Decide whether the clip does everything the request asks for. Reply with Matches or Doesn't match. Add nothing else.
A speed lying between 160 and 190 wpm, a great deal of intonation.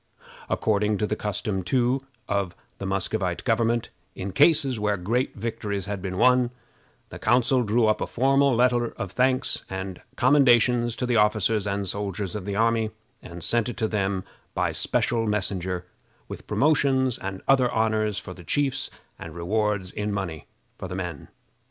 Doesn't match